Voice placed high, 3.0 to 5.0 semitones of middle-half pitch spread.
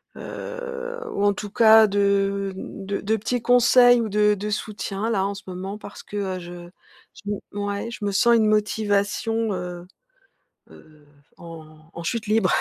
No: high, 205 Hz; narrow, 2.4 semitones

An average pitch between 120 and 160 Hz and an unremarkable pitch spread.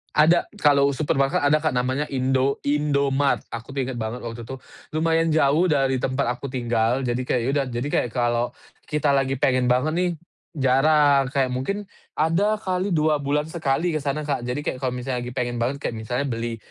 Yes: low, 135 Hz; average, 3.1 semitones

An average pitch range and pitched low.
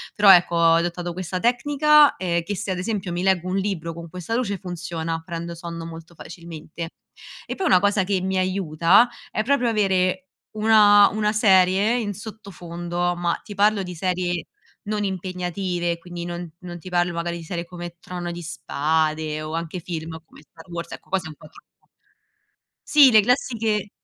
No: average, 3.1 semitones; medium, 180 Hz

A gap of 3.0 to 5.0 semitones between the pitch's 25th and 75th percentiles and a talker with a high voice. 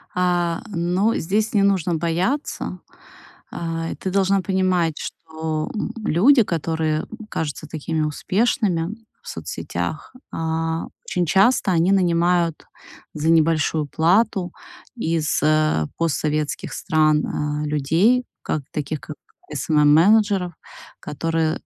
No: average, 3.3 semitones; medium, 165 Hz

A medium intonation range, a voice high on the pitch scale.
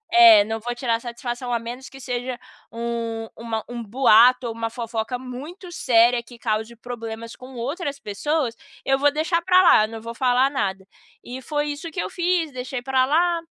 Yes: average, 3.5 semitones; high, 245 Hz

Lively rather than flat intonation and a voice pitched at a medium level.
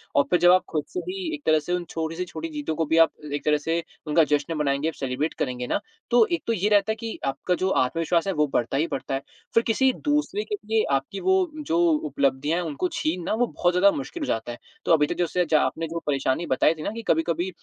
Yes: wide, 6.7 semitones; medium, 170 Hz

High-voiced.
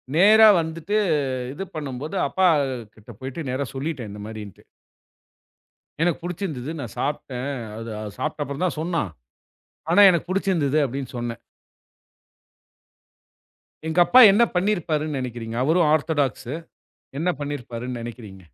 No: medium, 145 Hz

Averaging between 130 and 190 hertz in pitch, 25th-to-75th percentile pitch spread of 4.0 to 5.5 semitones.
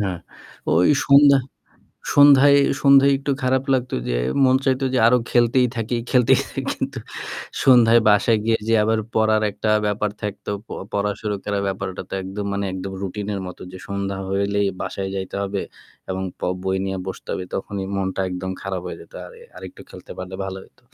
No: low, 105 Hz; average, 4.7 semitones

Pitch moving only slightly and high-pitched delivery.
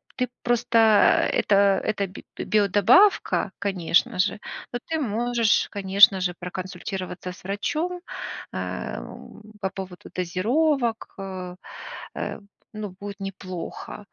No: average, 3.9 semitones; high, 200 Hz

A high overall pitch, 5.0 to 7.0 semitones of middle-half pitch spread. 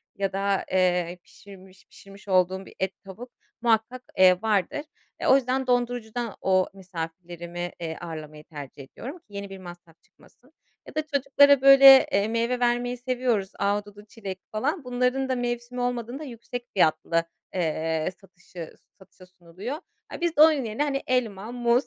Yes: high, 210 Hz; average, 5.3 semitones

